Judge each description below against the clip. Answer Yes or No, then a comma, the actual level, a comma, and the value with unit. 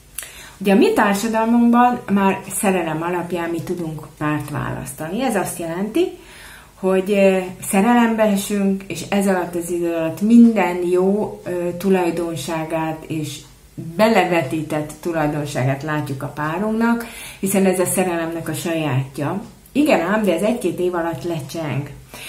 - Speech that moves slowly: No, average, 125 wpm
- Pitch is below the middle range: No, medium, 175 Hz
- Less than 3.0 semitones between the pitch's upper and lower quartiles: No, average, 4.0 semitones